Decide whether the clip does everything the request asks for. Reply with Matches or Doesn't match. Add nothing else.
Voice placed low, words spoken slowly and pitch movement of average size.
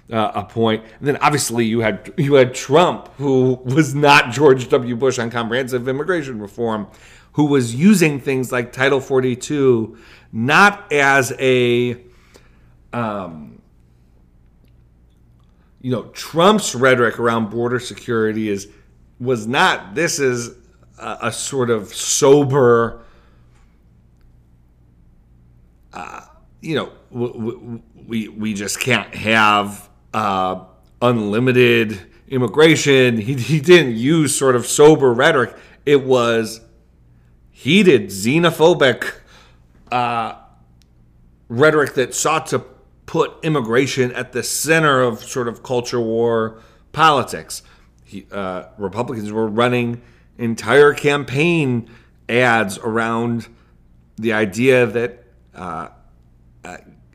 Doesn't match